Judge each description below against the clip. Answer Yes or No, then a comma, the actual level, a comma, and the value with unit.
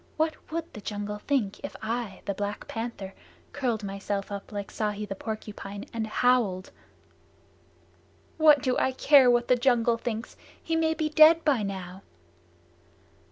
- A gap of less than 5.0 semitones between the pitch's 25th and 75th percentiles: Yes, average, 4.6 semitones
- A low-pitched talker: No, high, 225 Hz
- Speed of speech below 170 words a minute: Yes, average, 150 wpm